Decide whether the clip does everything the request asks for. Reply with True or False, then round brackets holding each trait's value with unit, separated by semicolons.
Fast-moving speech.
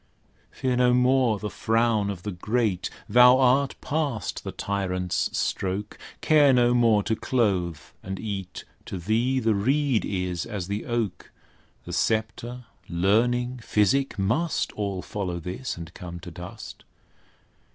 False (140 wpm)